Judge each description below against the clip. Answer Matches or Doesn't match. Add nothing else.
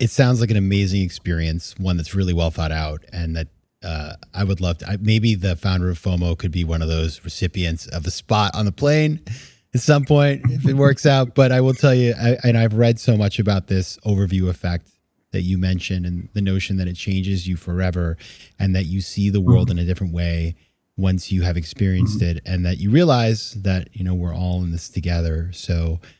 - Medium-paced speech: Doesn't match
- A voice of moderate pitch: Doesn't match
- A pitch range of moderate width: Matches